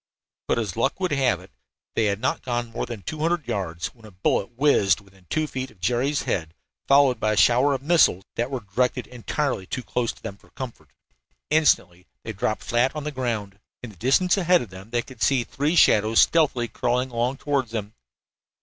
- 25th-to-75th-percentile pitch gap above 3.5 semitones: Yes, average, 4.7 semitones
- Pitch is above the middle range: No, low, 120 Hz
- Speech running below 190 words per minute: No, fast, 205 wpm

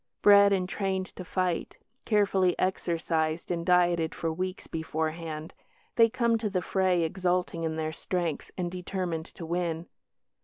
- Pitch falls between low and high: Yes, medium, 180 Hz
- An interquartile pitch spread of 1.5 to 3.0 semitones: Yes, narrow, 2.4 semitones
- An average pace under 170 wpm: Yes, average, 145 wpm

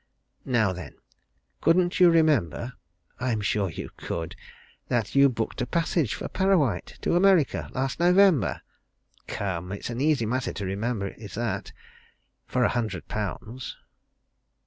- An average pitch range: No, wide, 7.4 semitones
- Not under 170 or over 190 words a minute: No, slow, 135 wpm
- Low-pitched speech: Yes, low, 120 Hz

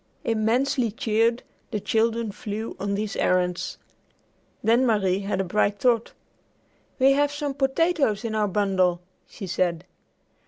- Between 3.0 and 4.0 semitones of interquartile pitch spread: Yes, average, 3.4 semitones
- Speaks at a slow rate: Yes, slow, 130 wpm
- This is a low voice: No, high, 215 Hz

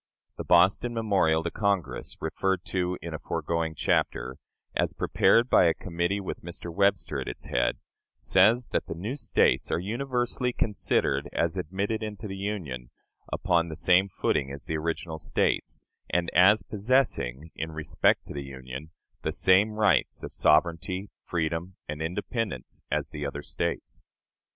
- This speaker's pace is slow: No, average, 155 wpm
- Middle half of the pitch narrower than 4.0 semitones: No, average, 4.3 semitones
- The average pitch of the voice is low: Yes, very low, 90 Hz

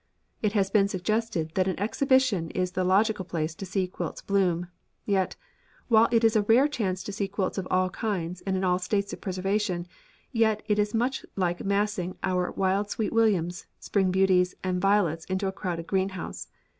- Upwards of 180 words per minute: Yes, average, 190 wpm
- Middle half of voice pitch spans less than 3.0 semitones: Yes, narrow, 2.5 semitones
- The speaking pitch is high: Yes, high, 195 Hz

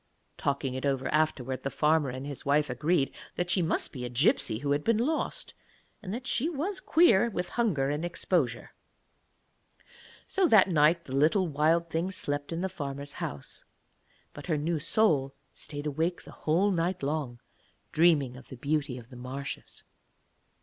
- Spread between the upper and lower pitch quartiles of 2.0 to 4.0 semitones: No, average, 4.5 semitones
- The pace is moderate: Yes, average, 170 wpm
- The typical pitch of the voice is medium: Yes, medium, 155 Hz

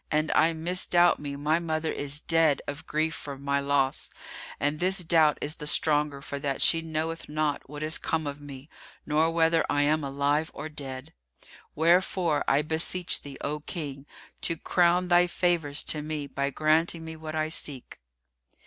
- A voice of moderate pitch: Yes, medium, 155 Hz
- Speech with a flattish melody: Yes, narrow, 2.2 semitones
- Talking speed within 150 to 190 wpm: Yes, average, 175 wpm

